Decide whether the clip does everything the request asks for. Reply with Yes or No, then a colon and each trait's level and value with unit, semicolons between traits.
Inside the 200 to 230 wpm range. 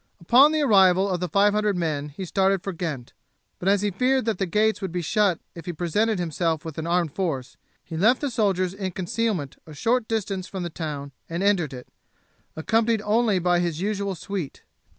Yes: fast, 205 wpm